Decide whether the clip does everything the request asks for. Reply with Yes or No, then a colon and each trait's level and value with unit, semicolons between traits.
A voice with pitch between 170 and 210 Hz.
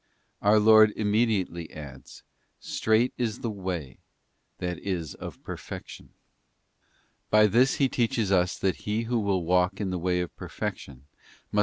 No: low, 100 Hz